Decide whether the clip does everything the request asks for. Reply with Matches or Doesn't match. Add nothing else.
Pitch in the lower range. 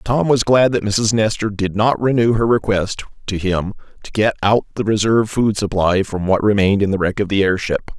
Matches